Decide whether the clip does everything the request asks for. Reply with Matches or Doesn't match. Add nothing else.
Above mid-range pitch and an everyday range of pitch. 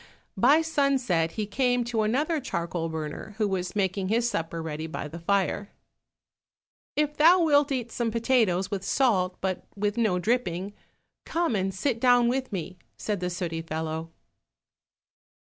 Doesn't match